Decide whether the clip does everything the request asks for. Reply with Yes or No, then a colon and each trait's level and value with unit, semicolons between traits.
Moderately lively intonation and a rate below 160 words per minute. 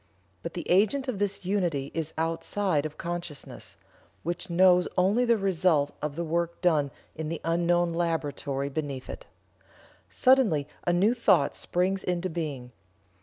Yes: average, 3.5 semitones; average, 145 wpm